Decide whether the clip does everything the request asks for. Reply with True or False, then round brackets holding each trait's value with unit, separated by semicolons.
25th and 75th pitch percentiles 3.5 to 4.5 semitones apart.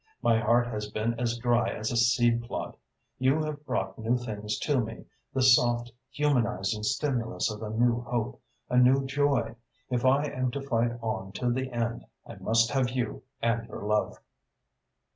False (2.4 semitones)